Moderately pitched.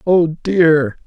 Yes: medium, 160 Hz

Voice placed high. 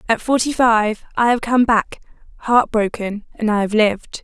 Yes: high, 225 Hz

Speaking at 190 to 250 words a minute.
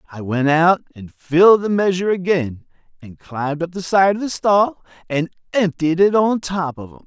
Yes: average, 195 wpm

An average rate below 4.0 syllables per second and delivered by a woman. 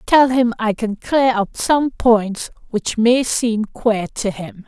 Yes: 3.3 syllables/s; female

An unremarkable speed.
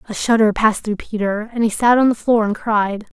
No: fast, 245 wpm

